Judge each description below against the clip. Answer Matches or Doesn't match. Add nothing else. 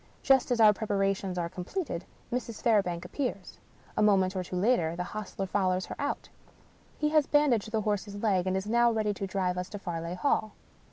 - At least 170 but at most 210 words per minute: Matches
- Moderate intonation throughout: Matches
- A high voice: Matches